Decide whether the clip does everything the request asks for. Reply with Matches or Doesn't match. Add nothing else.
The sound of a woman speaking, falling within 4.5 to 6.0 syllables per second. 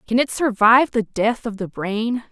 Matches